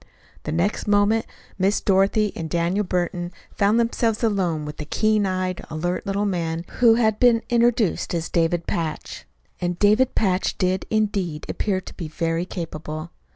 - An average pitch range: Yes, average, 3.9 semitones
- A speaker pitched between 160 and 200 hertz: Yes, medium, 185 Hz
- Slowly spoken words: No, average, 155 wpm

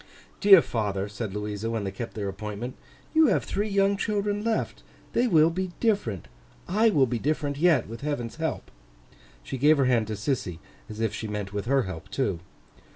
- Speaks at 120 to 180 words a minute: No, average, 190 wpm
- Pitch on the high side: No, low, 125 Hz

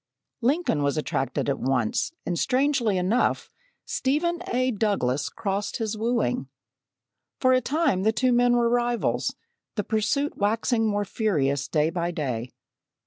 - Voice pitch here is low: No, high, 215 Hz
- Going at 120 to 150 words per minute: Yes, average, 140 wpm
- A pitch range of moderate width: No, wide, 7.1 semitones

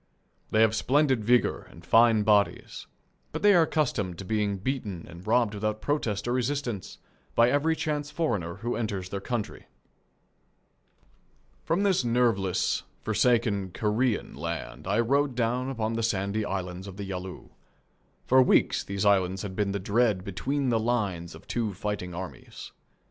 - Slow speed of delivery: No, average, 155 wpm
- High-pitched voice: No, low, 110 Hz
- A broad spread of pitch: No, average, 4.1 semitones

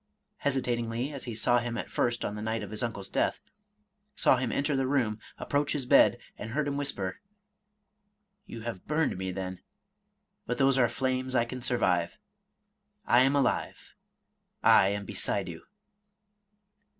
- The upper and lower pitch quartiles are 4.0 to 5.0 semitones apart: Yes, average, 4.5 semitones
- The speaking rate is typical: Yes, average, 175 wpm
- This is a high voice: No, low, 125 Hz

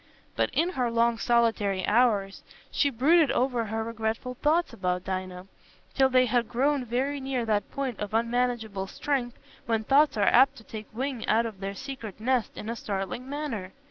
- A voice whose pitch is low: No, high, 235 Hz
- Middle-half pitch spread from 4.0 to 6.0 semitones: No, average, 3.6 semitones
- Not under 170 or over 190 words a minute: Yes, average, 175 wpm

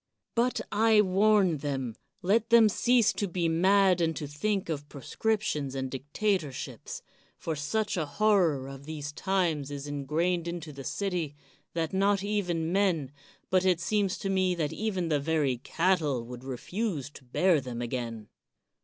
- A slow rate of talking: No, average, 155 wpm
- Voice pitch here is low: No, medium, 170 Hz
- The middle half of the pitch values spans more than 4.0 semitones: Yes, wide, 5.4 semitones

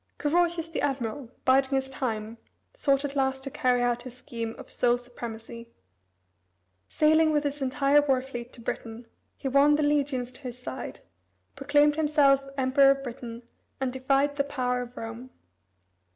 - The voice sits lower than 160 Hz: No, very high, 265 Hz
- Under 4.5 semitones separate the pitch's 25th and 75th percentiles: Yes, average, 2.8 semitones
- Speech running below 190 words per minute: Yes, average, 160 wpm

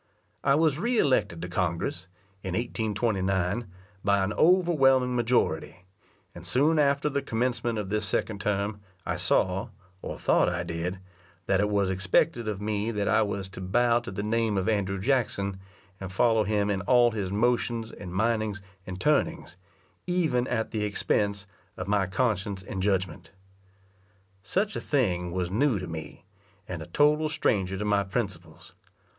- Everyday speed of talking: Yes, average, 160 wpm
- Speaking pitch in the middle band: No, low, 105 Hz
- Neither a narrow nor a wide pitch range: Yes, average, 4.4 semitones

